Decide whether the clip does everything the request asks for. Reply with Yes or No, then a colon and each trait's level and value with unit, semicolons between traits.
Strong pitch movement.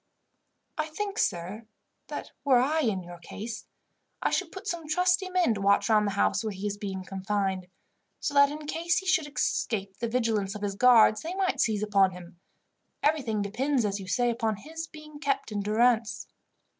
Yes: wide, 7.0 semitones